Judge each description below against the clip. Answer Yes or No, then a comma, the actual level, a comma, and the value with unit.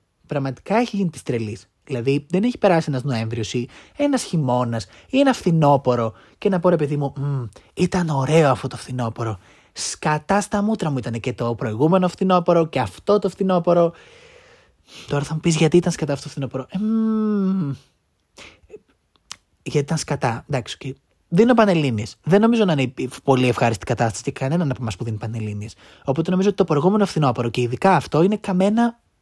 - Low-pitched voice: No, medium, 150 Hz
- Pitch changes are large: Yes, wide, 7.2 semitones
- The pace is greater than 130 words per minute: Yes, fast, 170 wpm